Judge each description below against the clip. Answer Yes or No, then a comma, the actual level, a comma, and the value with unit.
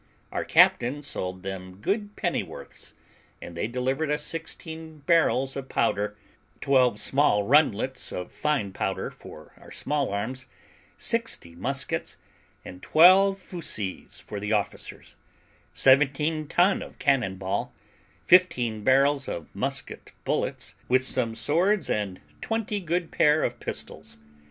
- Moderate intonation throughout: No, wide, 7.3 semitones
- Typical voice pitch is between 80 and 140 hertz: Yes, low, 135 Hz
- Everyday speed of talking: No, slow, 125 wpm